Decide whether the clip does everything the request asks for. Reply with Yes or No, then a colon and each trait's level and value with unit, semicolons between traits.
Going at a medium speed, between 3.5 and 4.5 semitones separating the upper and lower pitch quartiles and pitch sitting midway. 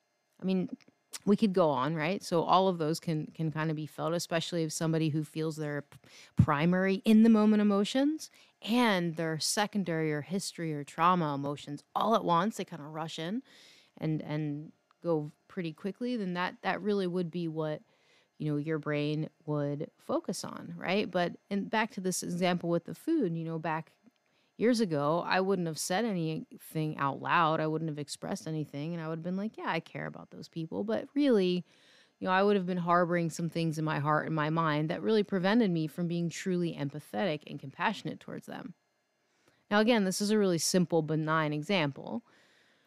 Yes: average, 195 wpm; average, 4.2 semitones; medium, 170 Hz